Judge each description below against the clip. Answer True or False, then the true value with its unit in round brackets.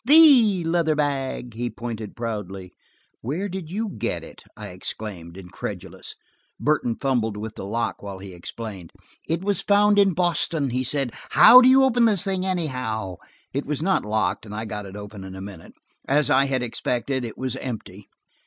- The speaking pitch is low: True (125 Hz)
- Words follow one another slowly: False (180 wpm)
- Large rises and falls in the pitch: True (8.8 semitones)